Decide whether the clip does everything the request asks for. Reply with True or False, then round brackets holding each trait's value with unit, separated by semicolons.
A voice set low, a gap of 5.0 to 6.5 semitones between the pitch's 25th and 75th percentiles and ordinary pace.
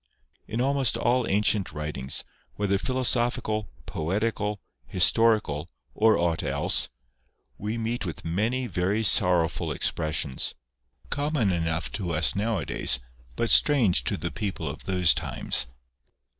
False (100 Hz; 5.5 semitones; 115 wpm)